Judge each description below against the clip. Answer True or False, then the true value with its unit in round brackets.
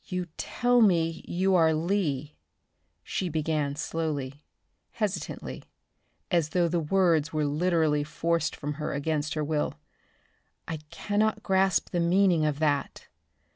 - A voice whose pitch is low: False (165 Hz)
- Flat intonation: False (3.3 semitones)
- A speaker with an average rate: False (130 wpm)